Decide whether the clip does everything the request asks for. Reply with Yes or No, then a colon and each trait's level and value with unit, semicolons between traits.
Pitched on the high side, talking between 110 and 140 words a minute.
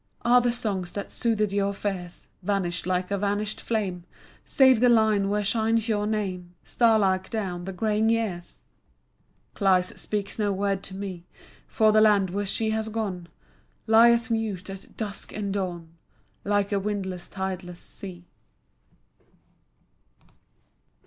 Yes: high, 200 Hz; slow, 135 wpm